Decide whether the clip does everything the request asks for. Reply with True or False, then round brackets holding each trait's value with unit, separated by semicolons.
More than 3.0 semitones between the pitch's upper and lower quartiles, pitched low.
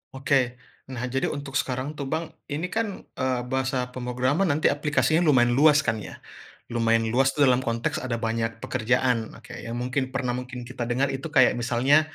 False (2.6 semitones; 130 Hz)